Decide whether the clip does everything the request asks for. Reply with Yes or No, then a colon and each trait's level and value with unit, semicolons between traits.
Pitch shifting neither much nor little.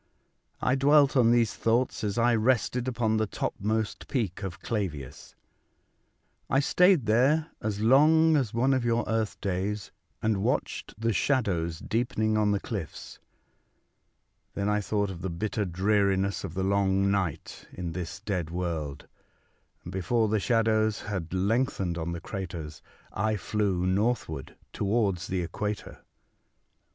Yes: average, 3.8 semitones